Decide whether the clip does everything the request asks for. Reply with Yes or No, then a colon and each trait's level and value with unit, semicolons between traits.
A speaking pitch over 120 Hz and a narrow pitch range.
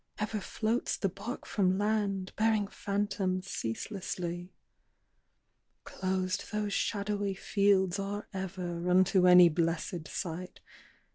Yes: high, 190 Hz; narrow, 2.1 semitones